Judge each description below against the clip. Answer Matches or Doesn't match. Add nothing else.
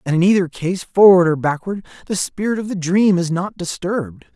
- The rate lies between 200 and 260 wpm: Matches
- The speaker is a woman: Doesn't match